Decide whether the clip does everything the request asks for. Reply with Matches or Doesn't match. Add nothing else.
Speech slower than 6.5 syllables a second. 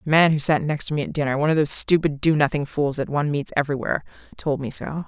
Doesn't match